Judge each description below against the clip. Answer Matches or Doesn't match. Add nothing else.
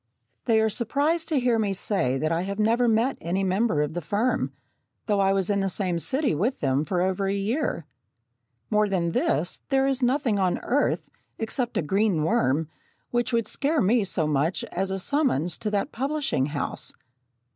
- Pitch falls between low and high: Doesn't match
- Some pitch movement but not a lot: Doesn't match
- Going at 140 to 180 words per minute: Doesn't match